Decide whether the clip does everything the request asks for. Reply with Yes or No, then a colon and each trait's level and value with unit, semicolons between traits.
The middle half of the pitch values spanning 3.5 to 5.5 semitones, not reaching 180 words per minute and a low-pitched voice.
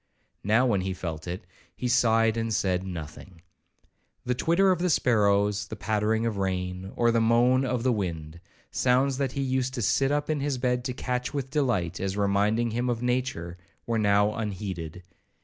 No: average, 4.8 semitones; average, 185 wpm; low, 115 Hz